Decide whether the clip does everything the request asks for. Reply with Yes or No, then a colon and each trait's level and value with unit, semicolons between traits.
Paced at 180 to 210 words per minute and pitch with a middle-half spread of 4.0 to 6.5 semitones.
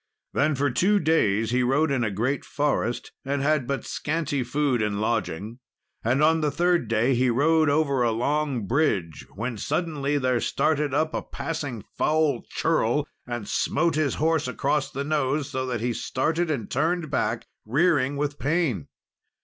No: average, 165 wpm; average, 4.3 semitones